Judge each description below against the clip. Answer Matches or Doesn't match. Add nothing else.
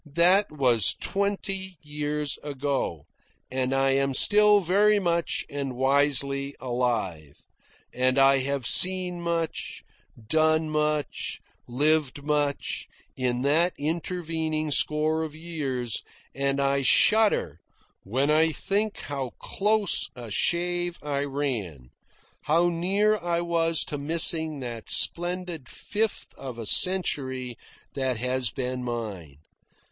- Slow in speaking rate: Matches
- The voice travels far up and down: Doesn't match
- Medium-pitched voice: Matches